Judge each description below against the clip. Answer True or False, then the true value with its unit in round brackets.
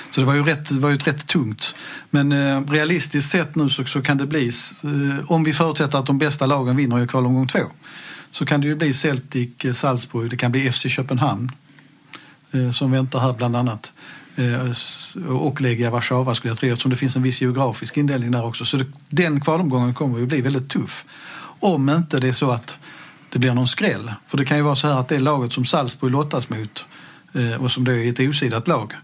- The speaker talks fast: True (220 wpm)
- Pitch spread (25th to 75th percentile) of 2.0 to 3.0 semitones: True (2.7 semitones)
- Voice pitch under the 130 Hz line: False (135 Hz)